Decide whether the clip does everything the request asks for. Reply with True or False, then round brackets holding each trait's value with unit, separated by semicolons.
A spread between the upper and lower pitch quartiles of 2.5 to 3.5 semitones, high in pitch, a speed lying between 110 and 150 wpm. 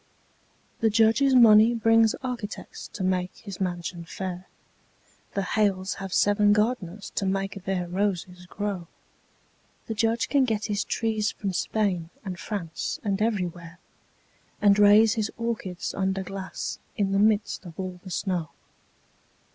True (2.8 semitones; 200 Hz; 140 wpm)